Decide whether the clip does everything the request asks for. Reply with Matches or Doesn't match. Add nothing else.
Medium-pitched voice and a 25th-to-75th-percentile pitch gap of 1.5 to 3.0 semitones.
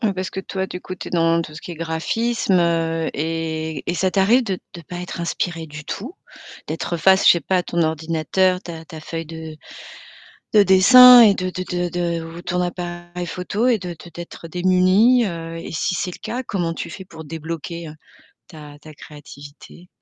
Matches